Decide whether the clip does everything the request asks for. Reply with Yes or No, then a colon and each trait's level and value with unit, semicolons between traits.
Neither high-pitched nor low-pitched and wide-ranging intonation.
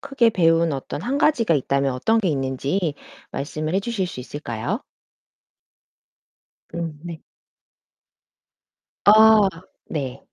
Yes: medium, 165 Hz; wide, 7.5 semitones